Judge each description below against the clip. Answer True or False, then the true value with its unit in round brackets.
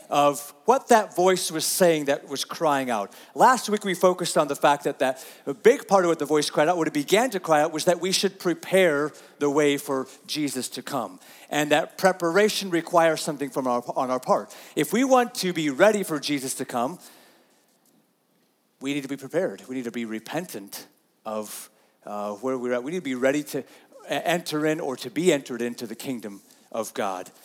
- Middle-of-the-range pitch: True (150 Hz)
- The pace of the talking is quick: True (210 wpm)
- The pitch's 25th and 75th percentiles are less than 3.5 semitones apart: False (5.2 semitones)